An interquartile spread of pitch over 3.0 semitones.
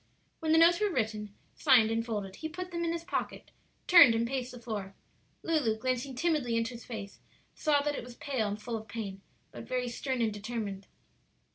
Yes: average, 5.0 semitones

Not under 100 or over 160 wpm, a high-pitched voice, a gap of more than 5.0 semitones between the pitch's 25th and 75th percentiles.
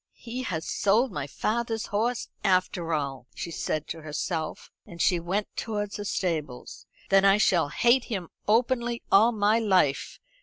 Yes: average, 155 wpm; high, 195 Hz; wide, 5.5 semitones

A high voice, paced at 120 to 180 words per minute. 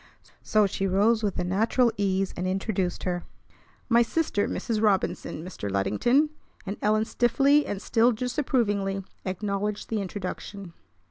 Yes: high, 205 Hz; slow, 135 wpm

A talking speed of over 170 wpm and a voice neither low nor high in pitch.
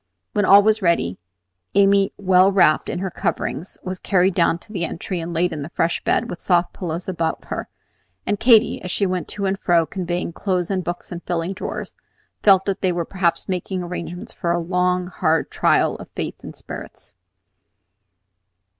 Yes: average, 185 wpm; medium, 180 Hz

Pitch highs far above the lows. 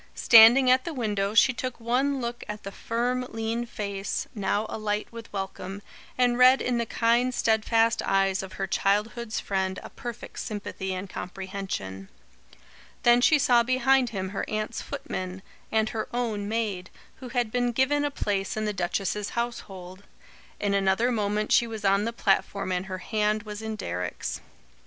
No: average, 3.4 semitones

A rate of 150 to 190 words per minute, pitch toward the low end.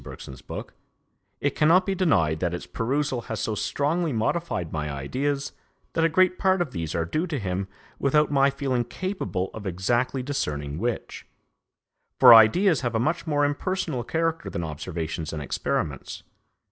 Yes: average, 160 wpm; low, 130 Hz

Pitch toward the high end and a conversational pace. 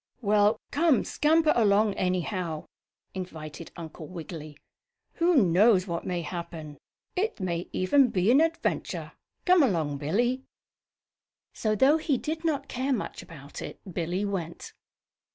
No: high, 200 Hz; slow, 130 wpm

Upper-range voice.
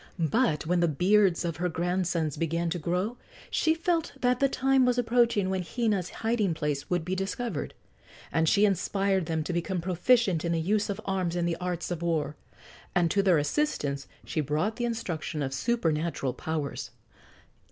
No: medium, 180 Hz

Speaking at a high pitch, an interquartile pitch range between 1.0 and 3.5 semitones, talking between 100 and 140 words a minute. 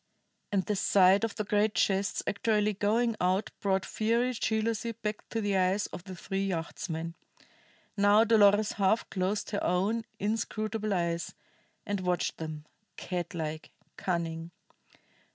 Yes: high, 200 Hz; average, 3.0 semitones; slow, 135 wpm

